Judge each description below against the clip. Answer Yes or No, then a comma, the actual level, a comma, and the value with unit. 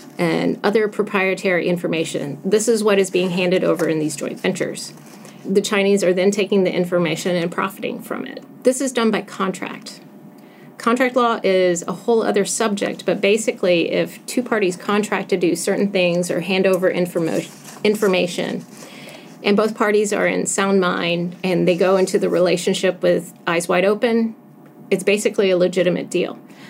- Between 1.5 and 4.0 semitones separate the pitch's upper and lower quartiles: Yes, average, 2.9 semitones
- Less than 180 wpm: Yes, average, 170 wpm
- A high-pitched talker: Yes, high, 195 Hz